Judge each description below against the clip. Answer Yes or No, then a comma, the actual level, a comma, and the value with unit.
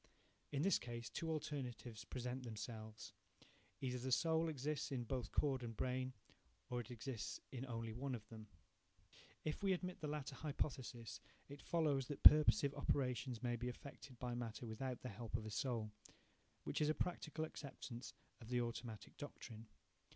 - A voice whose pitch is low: Yes, low, 125 Hz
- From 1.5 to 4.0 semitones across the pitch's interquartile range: Yes, average, 3.5 semitones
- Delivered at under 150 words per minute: No, average, 160 wpm